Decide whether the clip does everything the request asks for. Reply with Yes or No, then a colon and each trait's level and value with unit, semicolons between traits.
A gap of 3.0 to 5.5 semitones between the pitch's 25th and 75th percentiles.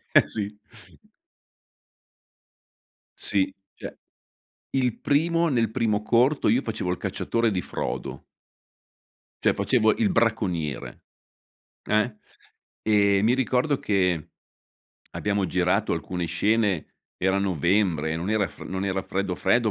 Yes: average, 3.7 semitones